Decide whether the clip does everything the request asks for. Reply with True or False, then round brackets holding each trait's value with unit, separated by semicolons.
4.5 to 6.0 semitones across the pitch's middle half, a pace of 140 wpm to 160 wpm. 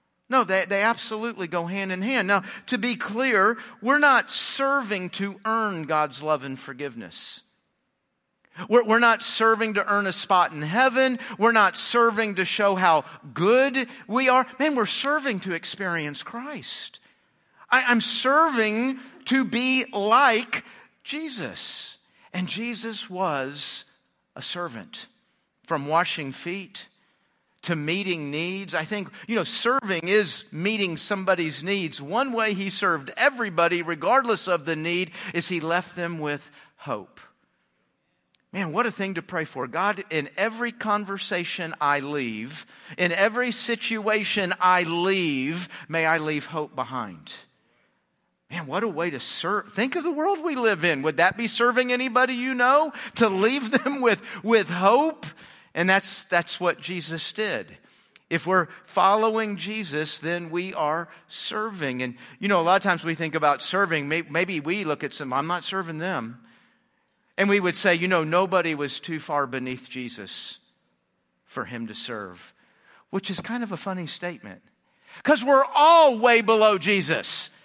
True (5.6 semitones; 155 wpm)